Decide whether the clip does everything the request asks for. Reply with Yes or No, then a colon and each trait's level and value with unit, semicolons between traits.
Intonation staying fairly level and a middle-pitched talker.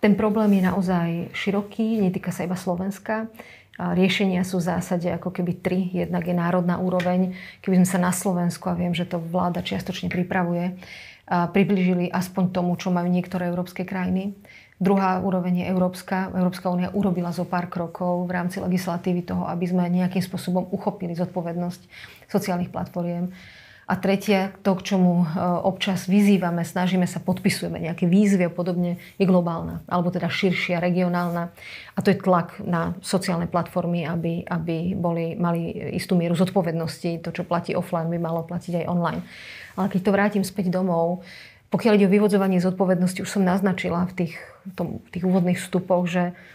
Yes: narrow, 1.4 semitones; medium, 180 Hz